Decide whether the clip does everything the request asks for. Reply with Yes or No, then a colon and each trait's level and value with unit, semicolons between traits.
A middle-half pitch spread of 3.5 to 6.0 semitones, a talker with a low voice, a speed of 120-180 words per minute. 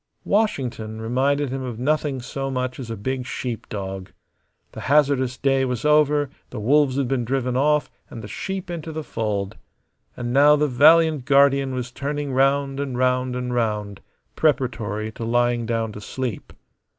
No: average, 3.0 semitones; low, 130 Hz; average, 165 wpm